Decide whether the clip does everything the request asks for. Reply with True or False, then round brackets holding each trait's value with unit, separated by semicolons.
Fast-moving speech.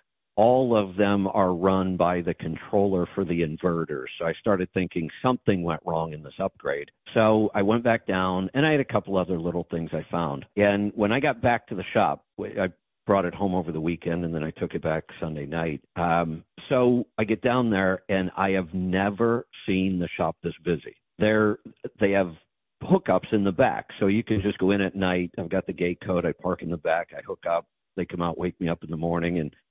True (225 wpm)